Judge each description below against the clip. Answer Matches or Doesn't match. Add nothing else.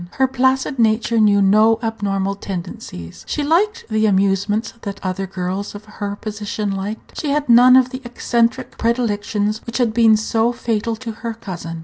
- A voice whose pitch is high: Matches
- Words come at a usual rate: Matches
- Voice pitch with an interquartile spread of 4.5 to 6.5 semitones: Doesn't match